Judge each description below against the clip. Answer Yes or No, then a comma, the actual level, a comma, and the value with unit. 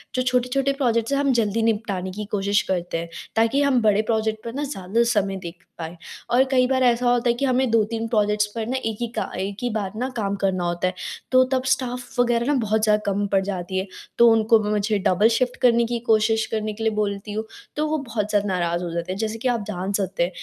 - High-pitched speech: Yes, high, 220 Hz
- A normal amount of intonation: Yes, average, 3.4 semitones